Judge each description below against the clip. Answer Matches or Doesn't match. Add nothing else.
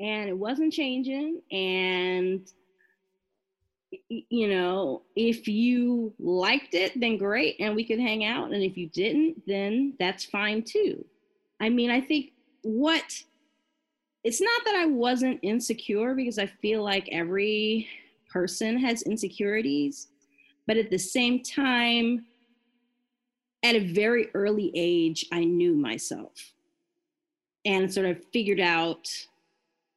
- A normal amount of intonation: Doesn't match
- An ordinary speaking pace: Doesn't match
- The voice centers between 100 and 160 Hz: Doesn't match